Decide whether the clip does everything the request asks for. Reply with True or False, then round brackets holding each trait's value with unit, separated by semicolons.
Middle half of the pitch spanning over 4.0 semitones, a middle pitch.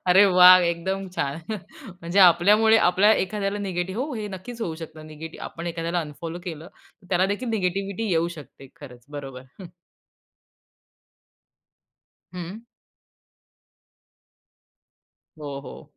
False (3.4 semitones; 180 Hz)